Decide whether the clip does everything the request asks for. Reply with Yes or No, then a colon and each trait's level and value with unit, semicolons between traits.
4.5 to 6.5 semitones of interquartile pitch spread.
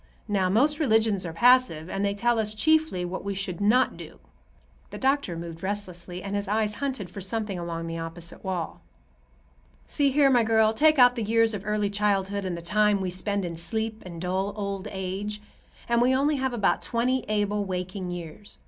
No: average, 3.7 semitones